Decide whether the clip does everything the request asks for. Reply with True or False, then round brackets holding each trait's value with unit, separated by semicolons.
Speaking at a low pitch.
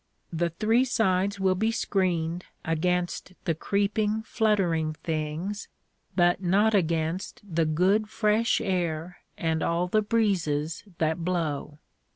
False (180 Hz)